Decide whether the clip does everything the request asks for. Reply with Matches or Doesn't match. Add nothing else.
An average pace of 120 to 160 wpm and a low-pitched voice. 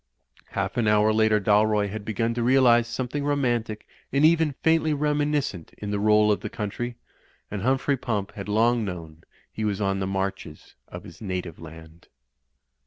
Doesn't match